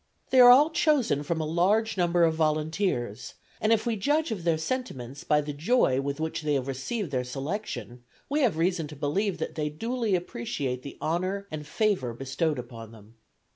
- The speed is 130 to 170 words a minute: No, average, 190 wpm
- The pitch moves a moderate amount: No, wide, 7.2 semitones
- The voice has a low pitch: No, medium, 160 Hz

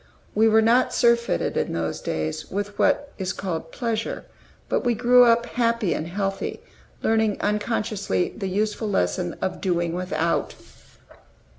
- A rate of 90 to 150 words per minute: Yes, average, 140 wpm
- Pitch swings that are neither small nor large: Yes, average, 4.4 semitones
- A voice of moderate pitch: No, high, 210 Hz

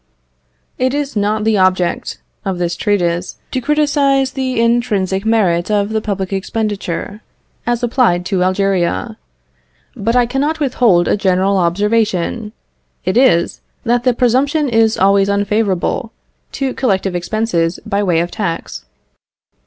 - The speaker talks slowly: Yes, slow, 130 wpm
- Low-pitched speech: No, high, 210 Hz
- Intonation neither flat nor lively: Yes, average, 4.4 semitones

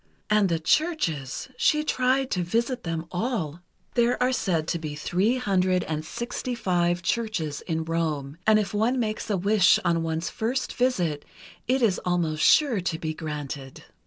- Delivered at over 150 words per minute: Yes, average, 160 wpm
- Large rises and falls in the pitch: Yes, wide, 6.7 semitones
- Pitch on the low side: No, medium, 180 Hz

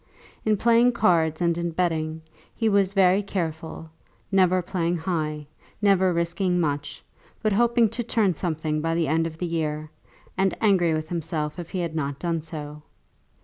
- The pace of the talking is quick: No, average, 165 wpm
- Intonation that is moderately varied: Yes, average, 3.3 semitones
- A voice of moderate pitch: Yes, medium, 170 Hz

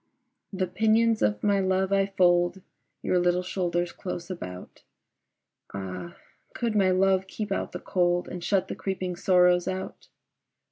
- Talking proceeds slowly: No, average, 145 wpm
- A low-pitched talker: No, medium, 185 Hz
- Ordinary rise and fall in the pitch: No, narrow, 1.7 semitones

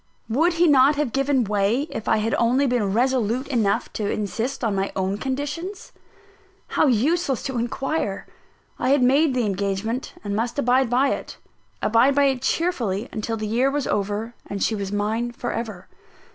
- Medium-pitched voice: No, high, 240 Hz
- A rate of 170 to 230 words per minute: Yes, average, 175 wpm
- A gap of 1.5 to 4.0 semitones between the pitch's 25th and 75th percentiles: No, average, 4.4 semitones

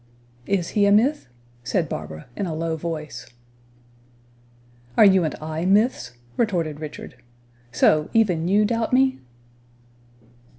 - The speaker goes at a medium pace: No, slow, 125 wpm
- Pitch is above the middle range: No, medium, 175 Hz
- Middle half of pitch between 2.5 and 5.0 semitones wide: No, wide, 5.4 semitones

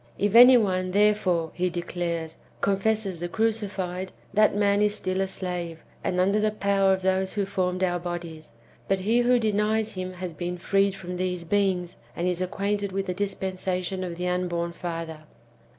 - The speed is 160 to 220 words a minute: Yes, average, 180 wpm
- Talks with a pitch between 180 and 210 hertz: Yes, medium, 185 Hz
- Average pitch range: No, narrow, 2.2 semitones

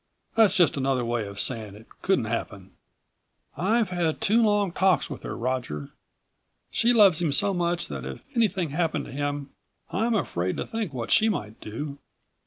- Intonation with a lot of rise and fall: Yes, wide, 8.6 semitones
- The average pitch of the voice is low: No, medium, 160 Hz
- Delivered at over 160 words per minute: Yes, average, 175 wpm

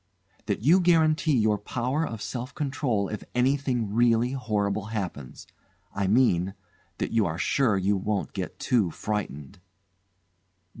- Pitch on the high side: No, low, 110 Hz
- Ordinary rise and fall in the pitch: Yes, average, 4.5 semitones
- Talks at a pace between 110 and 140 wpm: Yes, slow, 135 wpm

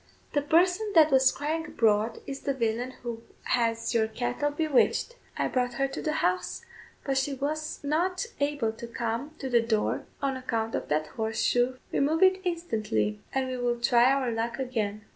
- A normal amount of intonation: Yes, average, 4.3 semitones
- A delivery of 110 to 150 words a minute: No, average, 180 wpm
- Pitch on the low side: No, very high, 255 Hz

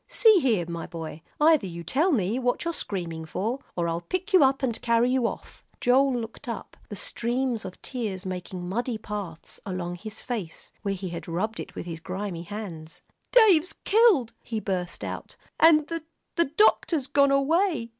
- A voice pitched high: Yes, high, 225 Hz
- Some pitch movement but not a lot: No, wide, 7.3 semitones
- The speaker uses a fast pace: No, average, 180 wpm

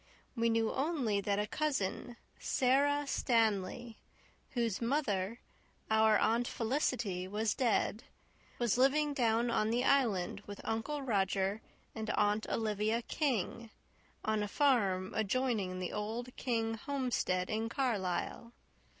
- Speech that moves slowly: Yes, slow, 120 wpm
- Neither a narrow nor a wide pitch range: Yes, average, 3.4 semitones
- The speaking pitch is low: No, high, 225 Hz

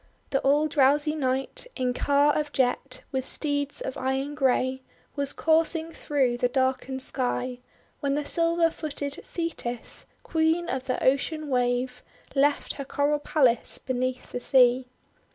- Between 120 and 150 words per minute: Yes, average, 140 wpm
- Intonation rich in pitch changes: No, narrow, 2.5 semitones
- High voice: Yes, very high, 275 Hz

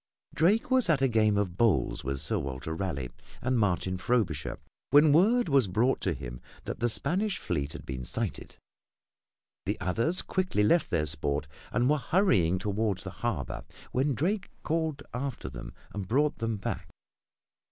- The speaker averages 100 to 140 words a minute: No, average, 165 wpm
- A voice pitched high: No, low, 110 Hz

